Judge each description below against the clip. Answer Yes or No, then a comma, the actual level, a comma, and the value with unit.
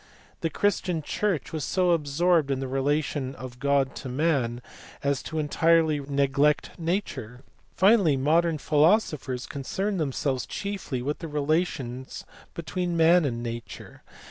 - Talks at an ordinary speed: No, slow, 130 wpm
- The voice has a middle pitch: Yes, medium, 150 Hz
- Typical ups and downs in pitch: Yes, average, 3.9 semitones